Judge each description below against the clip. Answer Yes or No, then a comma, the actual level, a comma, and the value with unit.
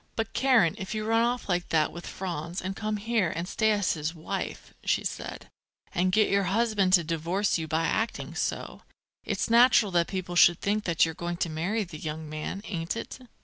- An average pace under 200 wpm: No, fast, 205 wpm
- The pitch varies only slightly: No, average, 4.3 semitones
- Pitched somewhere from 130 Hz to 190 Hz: Yes, medium, 185 Hz